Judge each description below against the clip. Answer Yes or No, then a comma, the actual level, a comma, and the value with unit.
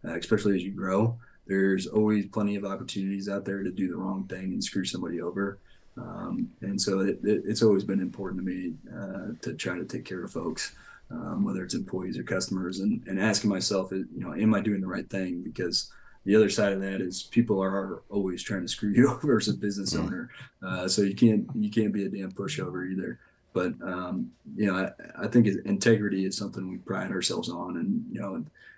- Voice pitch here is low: Yes, low, 100 Hz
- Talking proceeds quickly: Yes, fast, 220 wpm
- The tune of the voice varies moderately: No, narrow, 2.0 semitones